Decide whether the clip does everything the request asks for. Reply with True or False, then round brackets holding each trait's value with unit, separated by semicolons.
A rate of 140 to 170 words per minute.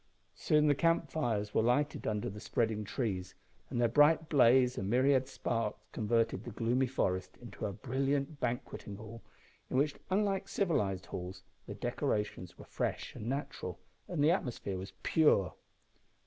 True (155 wpm)